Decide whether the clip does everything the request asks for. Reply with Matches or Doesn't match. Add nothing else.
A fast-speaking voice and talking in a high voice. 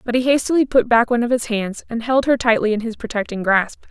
Matches